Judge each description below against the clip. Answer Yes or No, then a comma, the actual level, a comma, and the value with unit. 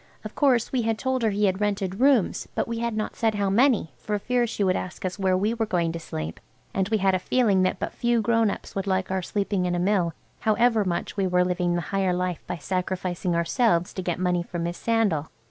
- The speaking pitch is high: Yes, high, 195 Hz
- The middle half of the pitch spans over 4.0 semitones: No, average, 3.7 semitones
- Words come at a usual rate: No, fast, 240 wpm